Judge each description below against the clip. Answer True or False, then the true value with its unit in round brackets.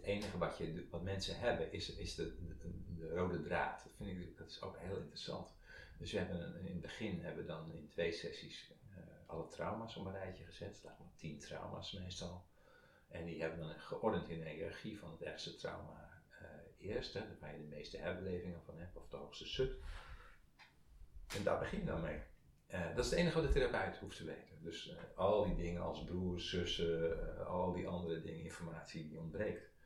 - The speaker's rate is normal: False (205 wpm)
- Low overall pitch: True (85 Hz)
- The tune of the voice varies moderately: False (2.1 semitones)